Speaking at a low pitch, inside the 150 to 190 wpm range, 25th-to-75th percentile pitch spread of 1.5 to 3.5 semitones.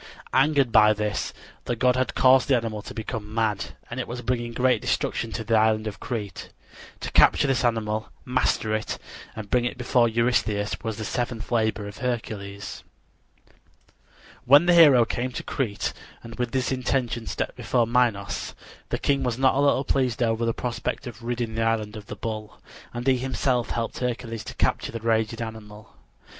Yes: low, 115 Hz; average, 180 wpm; narrow, 2.4 semitones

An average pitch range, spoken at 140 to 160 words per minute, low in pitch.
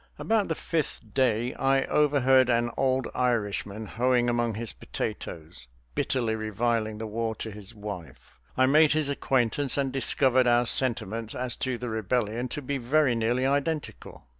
Yes: average, 3.3 semitones; average, 155 wpm; low, 120 Hz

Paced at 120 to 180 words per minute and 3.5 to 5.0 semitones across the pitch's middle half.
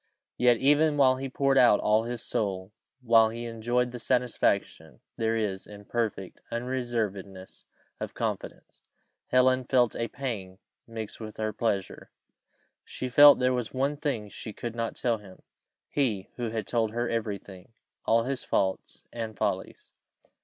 No: average, 155 wpm; average, 2.9 semitones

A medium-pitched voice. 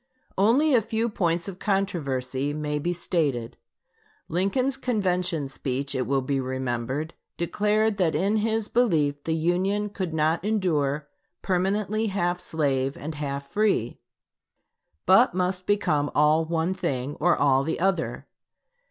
Yes: medium, 170 Hz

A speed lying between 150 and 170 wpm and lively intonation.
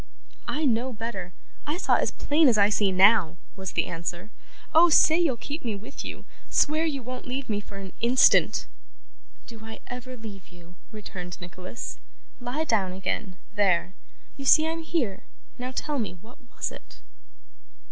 Yes: average, 165 wpm; wide, 6.3 semitones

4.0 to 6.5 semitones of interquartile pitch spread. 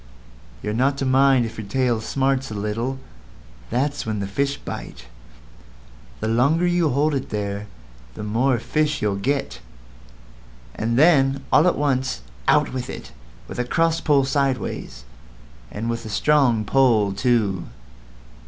Yes: average, 4.3 semitones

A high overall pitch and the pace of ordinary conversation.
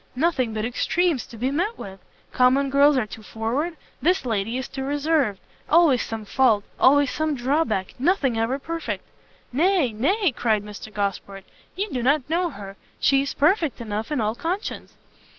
Yes: very high, 265 Hz; average, 170 wpm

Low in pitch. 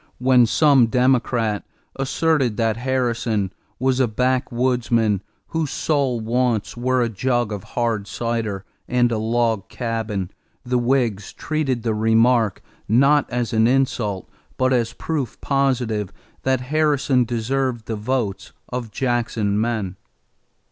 Yes: low, 120 Hz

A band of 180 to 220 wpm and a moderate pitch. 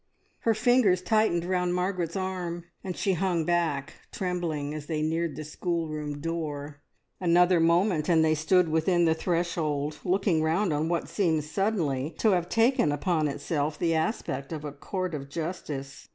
No: average, 160 wpm; medium, 165 Hz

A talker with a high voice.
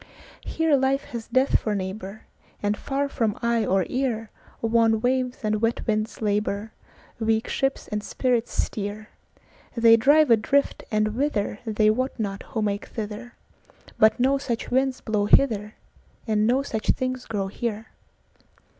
Yes: high, 225 Hz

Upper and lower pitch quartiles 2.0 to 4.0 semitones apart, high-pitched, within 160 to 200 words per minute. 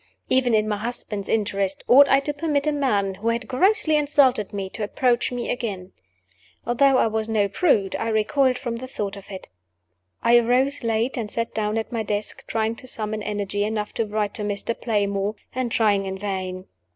Yes: average, 3.6 semitones; high, 220 Hz; average, 195 wpm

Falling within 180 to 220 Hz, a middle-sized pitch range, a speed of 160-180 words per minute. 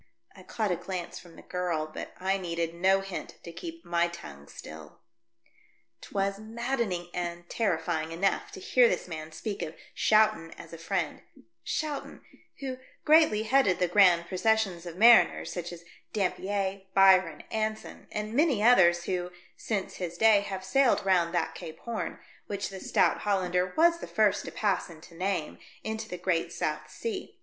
Yes: high, 190 Hz; average, 4.1 semitones; average, 175 wpm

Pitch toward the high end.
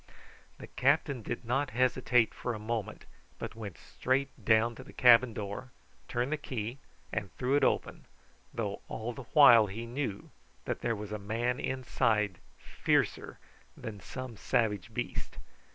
No: low, 115 Hz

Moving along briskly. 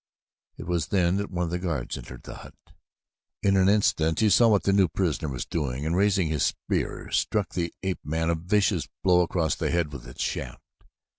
Yes: fast, 210 wpm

